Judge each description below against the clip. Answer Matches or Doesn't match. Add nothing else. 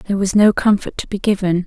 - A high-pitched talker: Matches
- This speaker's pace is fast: Matches